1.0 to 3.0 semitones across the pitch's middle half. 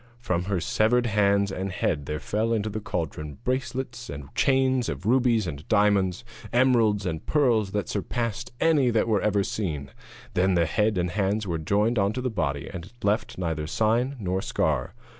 No: average, 4.7 semitones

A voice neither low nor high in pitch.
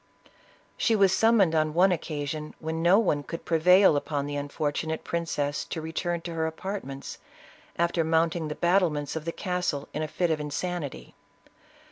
Yes: medium, 160 Hz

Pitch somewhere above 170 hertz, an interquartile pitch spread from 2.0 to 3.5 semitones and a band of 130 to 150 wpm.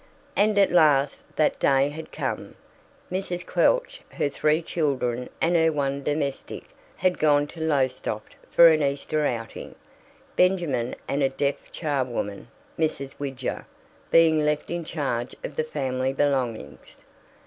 No: medium, 145 Hz; average, 3.2 semitones; slow, 135 wpm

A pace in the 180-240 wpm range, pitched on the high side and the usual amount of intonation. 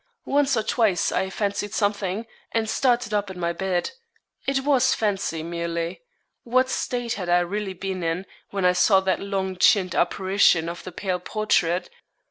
No: average, 165 wpm; high, 195 Hz; average, 3.4 semitones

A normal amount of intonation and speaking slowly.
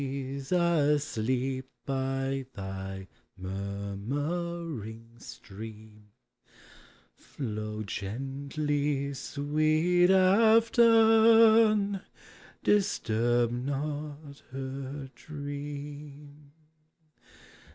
Yes: average, 4.7 semitones; slow, 45 wpm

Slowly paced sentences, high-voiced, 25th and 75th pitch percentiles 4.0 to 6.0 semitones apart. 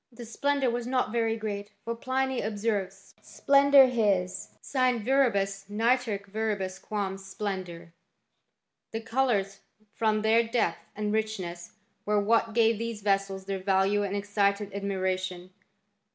No: slow, 130 wpm; high, 210 Hz; average, 2.9 semitones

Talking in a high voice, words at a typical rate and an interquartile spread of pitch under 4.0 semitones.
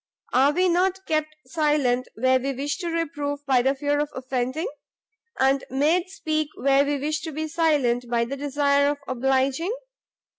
Yes: very high, 285 Hz; average, 170 wpm; average, 2.8 semitones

